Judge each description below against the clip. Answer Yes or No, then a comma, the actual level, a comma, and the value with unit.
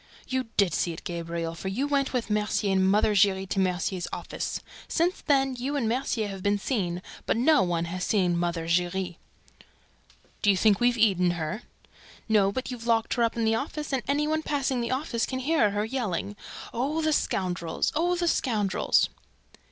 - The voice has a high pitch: Yes, high, 215 Hz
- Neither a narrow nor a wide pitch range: No, wide, 5.9 semitones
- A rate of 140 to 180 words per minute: No, average, 190 wpm